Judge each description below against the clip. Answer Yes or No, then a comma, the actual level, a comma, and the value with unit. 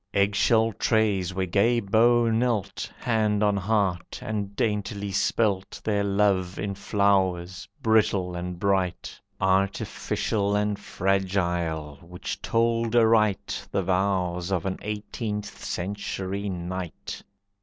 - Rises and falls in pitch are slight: Yes, narrow, 2.3 semitones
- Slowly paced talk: Yes, slow, 110 wpm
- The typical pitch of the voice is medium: No, low, 100 Hz